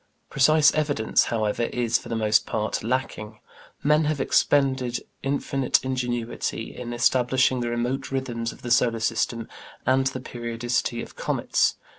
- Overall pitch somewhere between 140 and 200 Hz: No, low, 120 Hz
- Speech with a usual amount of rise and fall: No, narrow, 2.3 semitones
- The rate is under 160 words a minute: Yes, average, 140 wpm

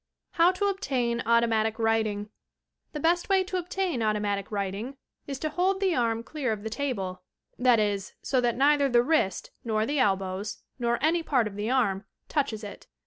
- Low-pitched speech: No, high, 235 Hz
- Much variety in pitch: Yes, wide, 5.8 semitones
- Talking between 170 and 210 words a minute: Yes, average, 185 wpm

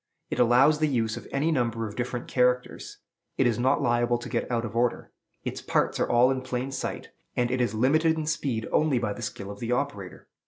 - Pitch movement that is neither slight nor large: No, narrow, 2.3 semitones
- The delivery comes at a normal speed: No, fast, 225 wpm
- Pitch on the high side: No, low, 125 Hz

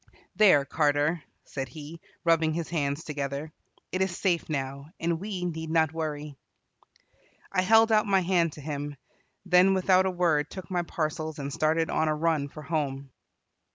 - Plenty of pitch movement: No, average, 3.3 semitones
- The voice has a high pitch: No, medium, 160 Hz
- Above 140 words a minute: Yes, average, 165 wpm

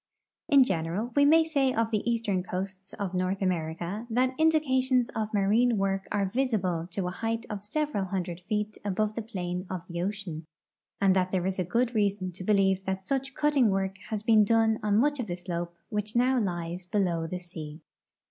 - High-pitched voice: Yes, high, 200 Hz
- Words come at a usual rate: Yes, average, 190 wpm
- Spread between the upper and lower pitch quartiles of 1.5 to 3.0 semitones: No, average, 4.0 semitones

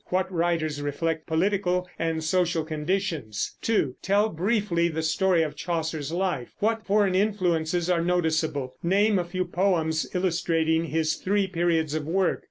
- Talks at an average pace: Yes, average, 145 wpm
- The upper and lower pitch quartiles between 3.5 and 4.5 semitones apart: No, average, 2.9 semitones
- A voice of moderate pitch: Yes, medium, 170 Hz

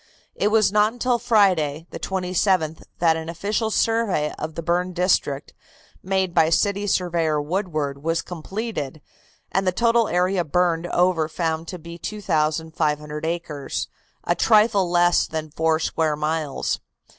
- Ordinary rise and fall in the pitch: Yes, average, 3.6 semitones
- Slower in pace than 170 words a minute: Yes, average, 140 wpm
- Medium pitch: Yes, medium, 175 Hz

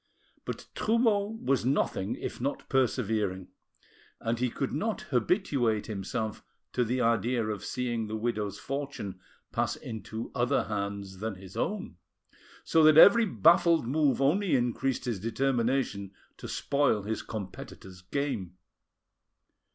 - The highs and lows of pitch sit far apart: No, average, 5.0 semitones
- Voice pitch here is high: No, low, 120 Hz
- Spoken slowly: Yes, slow, 130 wpm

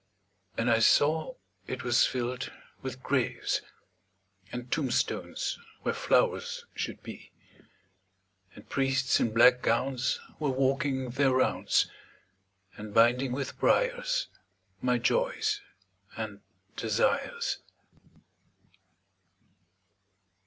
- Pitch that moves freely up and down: No, average, 4.6 semitones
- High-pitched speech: No, low, 135 Hz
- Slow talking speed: Yes, slow, 90 wpm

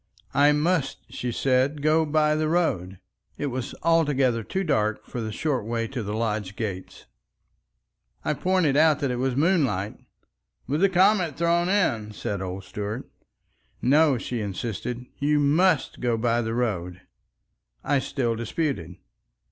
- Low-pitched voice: Yes, low, 130 Hz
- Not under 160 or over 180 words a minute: No, average, 150 wpm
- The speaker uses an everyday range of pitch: No, wide, 5.7 semitones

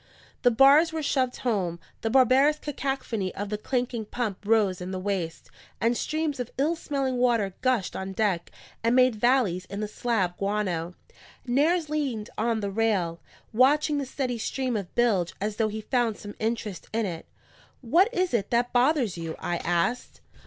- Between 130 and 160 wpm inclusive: No, average, 175 wpm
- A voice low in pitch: No, high, 230 Hz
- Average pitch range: Yes, average, 4.7 semitones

